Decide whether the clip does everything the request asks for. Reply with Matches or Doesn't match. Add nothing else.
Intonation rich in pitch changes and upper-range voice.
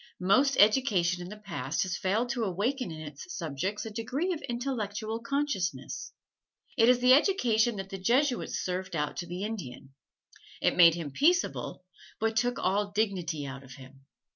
Matches